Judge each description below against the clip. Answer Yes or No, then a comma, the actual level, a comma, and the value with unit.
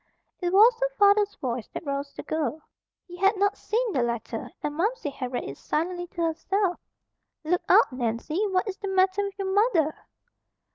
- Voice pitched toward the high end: Yes, very high, 360 Hz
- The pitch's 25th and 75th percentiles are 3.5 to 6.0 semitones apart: Yes, average, 5.3 semitones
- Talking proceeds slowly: No, average, 185 wpm